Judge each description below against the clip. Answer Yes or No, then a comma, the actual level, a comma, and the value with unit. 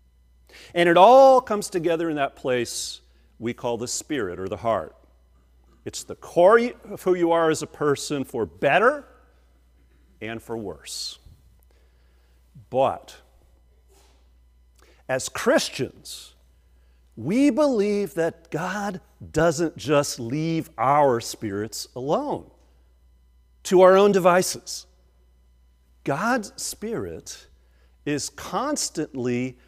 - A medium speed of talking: No, slow, 105 wpm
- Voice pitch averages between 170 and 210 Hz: No, low, 110 Hz